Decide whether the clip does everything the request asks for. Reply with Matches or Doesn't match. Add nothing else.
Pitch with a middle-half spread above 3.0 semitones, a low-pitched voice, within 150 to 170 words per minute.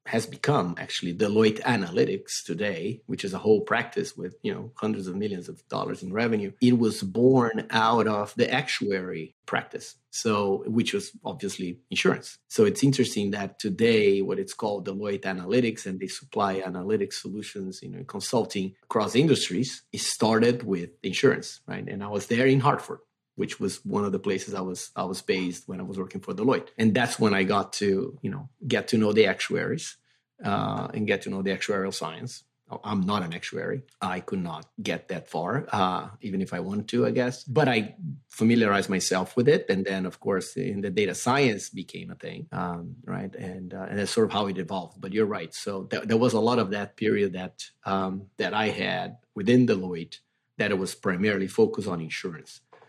Doesn't match